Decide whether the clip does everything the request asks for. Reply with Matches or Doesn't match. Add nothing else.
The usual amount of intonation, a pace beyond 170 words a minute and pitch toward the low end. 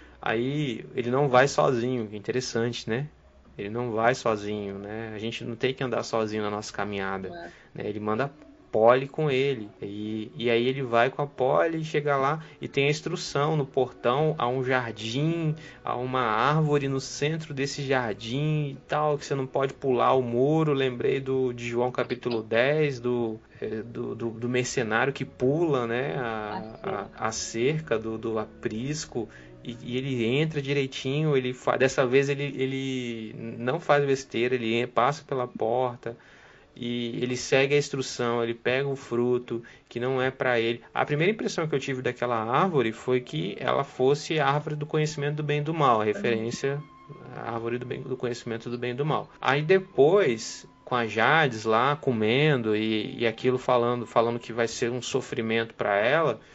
Matches